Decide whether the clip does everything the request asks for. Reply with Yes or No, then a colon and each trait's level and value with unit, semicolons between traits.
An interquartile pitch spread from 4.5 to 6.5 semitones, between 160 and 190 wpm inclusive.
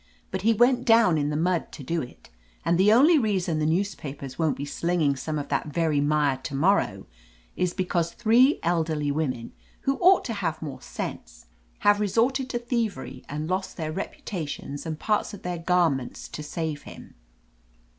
Yes: wide, 5.5 semitones; average, 180 wpm